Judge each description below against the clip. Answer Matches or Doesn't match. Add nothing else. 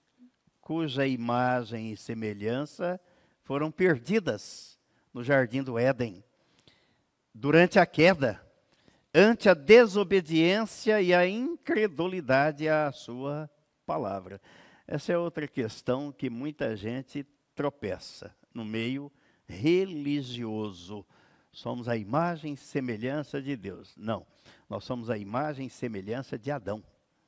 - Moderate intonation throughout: Doesn't match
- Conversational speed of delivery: Doesn't match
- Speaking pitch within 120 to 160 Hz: Matches